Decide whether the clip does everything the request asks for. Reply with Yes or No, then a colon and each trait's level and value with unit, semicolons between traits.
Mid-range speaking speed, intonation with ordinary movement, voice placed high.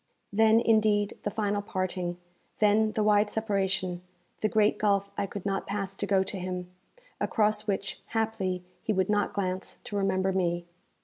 No: average, 165 wpm; narrow, 2.0 semitones; high, 200 Hz